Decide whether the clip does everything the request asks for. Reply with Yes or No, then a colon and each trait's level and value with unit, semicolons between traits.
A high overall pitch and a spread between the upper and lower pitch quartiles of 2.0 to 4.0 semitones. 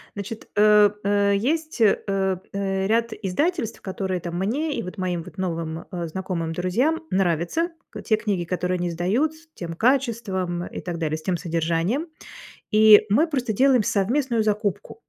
No: high, 200 Hz; average, 4.8 semitones